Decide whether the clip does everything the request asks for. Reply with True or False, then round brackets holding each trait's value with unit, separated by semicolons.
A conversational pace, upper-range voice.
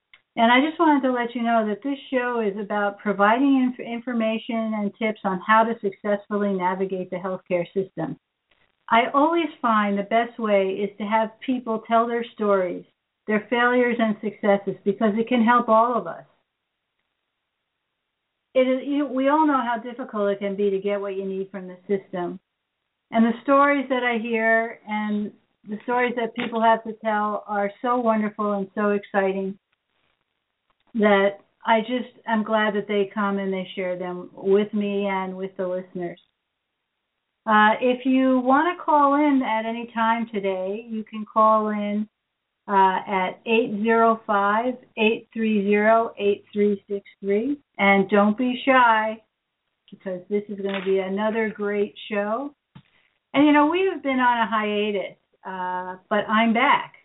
True (160 wpm; 215 Hz)